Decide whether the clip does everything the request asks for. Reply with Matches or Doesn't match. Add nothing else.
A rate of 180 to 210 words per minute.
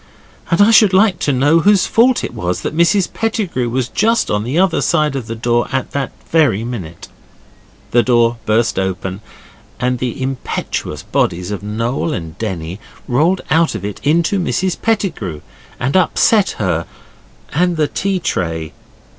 Doesn't match